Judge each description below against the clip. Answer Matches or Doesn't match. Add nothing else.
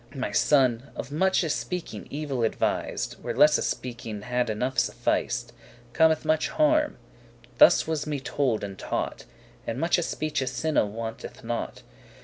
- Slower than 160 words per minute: Matches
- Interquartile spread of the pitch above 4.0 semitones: Matches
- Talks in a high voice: Doesn't match